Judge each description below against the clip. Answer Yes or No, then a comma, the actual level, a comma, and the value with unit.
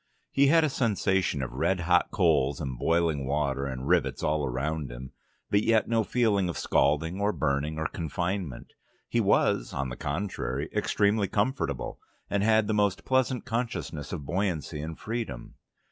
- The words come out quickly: No, average, 160 wpm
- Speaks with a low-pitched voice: Yes, very low, 85 Hz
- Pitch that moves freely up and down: Yes, wide, 6.5 semitones